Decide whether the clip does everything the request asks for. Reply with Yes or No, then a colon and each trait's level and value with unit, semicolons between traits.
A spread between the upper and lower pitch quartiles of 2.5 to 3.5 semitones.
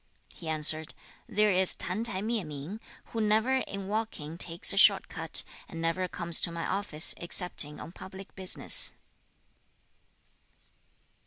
No: average, 4.0 semitones